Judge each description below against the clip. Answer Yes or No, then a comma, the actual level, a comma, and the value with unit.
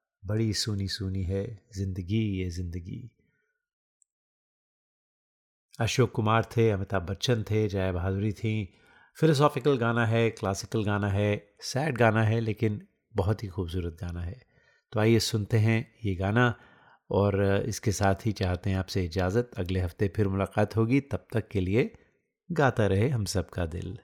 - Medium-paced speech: Yes, average, 145 wpm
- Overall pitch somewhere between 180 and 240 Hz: No, low, 105 Hz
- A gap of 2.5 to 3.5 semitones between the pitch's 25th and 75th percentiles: Yes, average, 3.2 semitones